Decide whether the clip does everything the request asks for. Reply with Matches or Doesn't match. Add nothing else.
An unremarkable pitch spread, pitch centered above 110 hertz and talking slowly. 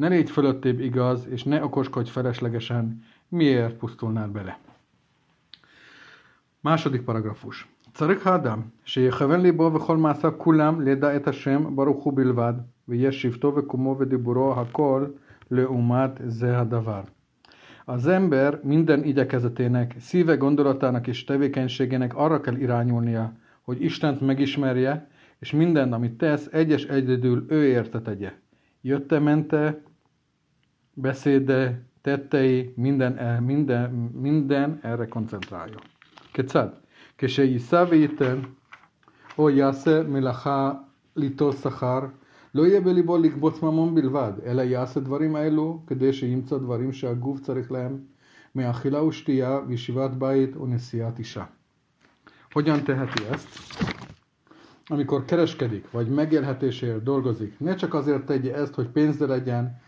Matches